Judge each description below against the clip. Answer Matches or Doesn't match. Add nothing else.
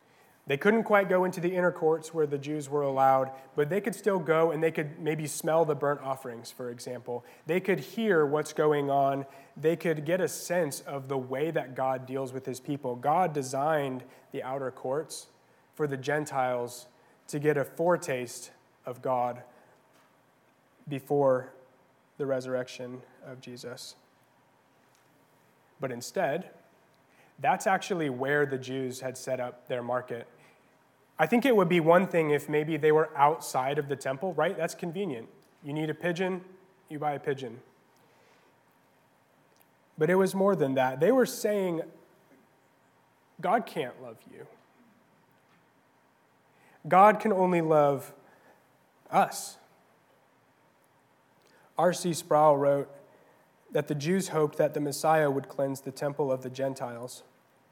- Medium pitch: Matches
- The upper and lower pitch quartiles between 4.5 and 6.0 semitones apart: Doesn't match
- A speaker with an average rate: Matches